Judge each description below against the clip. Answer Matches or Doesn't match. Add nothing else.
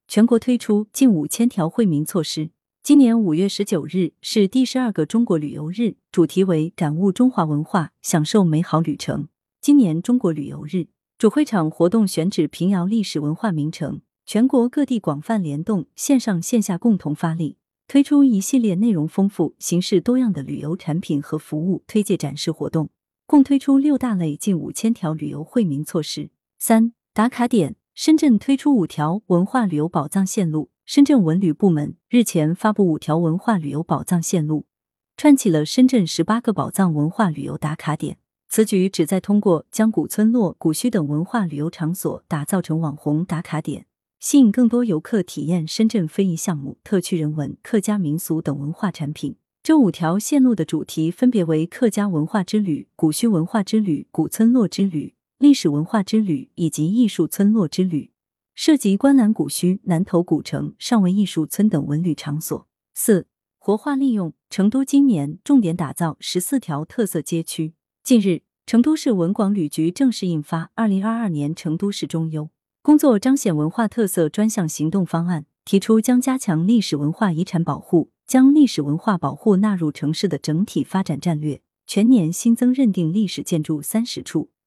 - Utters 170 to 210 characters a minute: Doesn't match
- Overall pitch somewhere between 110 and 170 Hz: Doesn't match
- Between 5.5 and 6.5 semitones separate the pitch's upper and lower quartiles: Matches